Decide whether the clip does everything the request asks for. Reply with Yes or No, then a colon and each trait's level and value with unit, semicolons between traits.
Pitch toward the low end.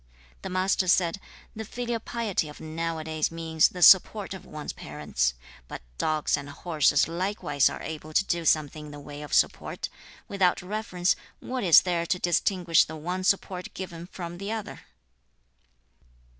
No: medium, 170 Hz